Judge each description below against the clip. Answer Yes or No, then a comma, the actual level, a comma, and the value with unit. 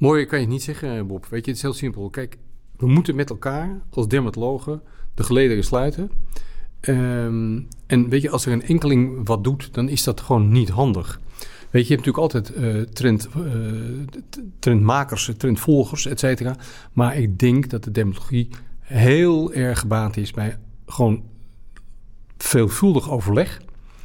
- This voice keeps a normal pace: Yes, average, 165 wpm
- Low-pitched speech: Yes, low, 125 Hz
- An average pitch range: Yes, average, 3.5 semitones